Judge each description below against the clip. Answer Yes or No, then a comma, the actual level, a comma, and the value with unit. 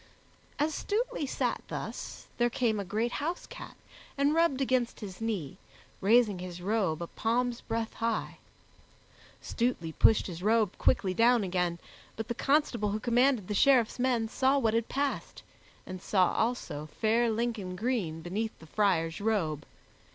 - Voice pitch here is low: No, high, 225 Hz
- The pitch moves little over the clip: No, average, 4.8 semitones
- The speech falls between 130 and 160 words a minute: Yes, average, 150 wpm